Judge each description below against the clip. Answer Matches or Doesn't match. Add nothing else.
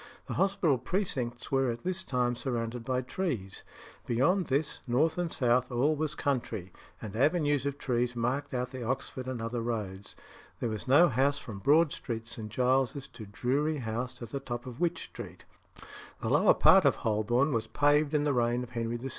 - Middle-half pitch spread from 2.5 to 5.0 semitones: Matches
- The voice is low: Matches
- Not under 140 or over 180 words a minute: Doesn't match